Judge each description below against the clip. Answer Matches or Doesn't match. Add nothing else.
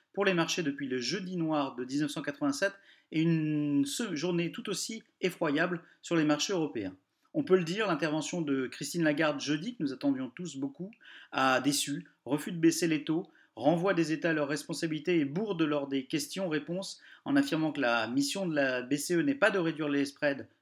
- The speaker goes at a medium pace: Matches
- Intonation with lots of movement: Doesn't match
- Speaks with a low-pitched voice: Doesn't match